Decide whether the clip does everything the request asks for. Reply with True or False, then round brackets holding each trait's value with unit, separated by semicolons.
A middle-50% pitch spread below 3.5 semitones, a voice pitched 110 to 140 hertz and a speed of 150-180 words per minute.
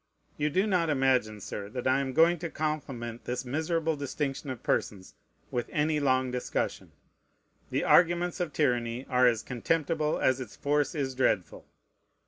False (4.0 semitones; 135 Hz; 155 wpm)